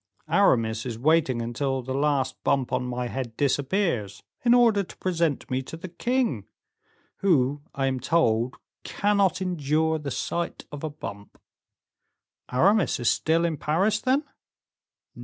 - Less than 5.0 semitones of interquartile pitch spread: No, wide, 5.6 semitones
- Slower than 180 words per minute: Yes, average, 140 wpm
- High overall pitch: No, medium, 145 Hz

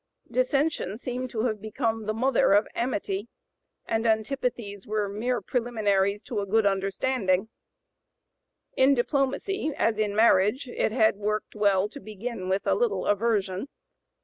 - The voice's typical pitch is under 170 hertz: No, high, 220 Hz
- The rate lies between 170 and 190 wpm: No, average, 140 wpm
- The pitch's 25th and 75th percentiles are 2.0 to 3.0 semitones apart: No, average, 3.5 semitones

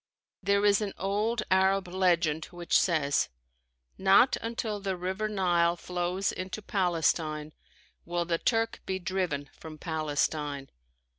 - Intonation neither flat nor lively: Yes, average, 3.2 semitones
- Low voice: No, medium, 180 Hz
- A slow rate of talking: Yes, slow, 125 wpm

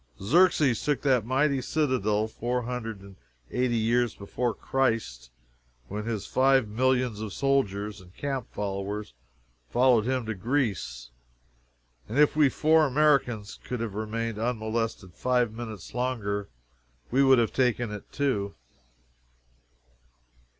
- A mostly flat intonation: No, average, 3.6 semitones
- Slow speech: Yes, slow, 125 wpm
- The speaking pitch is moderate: No, low, 115 Hz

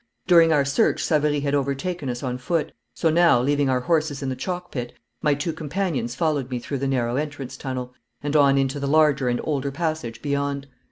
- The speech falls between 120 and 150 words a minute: No, fast, 205 wpm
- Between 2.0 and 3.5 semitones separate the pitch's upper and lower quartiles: Yes, average, 3.0 semitones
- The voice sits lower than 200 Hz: Yes, medium, 140 Hz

